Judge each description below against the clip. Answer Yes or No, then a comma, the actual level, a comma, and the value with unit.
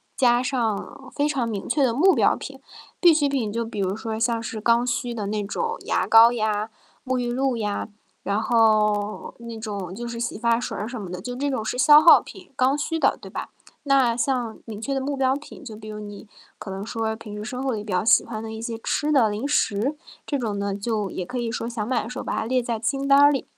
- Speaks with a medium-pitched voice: No, high, 230 Hz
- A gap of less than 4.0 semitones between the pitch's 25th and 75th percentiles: Yes, average, 3.4 semitones